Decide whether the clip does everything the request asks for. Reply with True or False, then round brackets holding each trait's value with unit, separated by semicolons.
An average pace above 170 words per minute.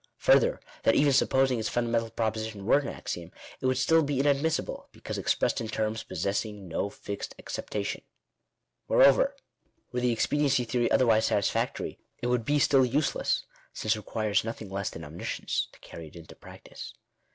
False (165 wpm)